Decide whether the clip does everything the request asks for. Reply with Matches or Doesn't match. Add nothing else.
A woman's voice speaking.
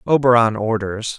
Doesn't match